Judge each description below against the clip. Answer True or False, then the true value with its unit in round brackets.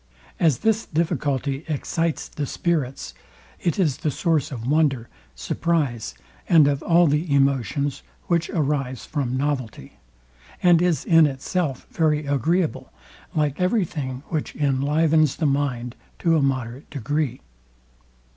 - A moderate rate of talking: False (125 wpm)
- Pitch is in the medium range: True (145 Hz)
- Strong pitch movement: False (3.4 semitones)